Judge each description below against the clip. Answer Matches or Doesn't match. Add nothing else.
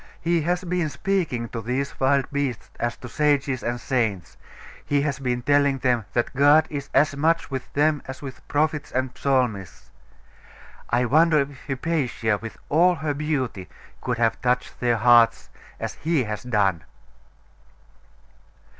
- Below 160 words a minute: Matches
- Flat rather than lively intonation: Doesn't match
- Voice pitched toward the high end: Doesn't match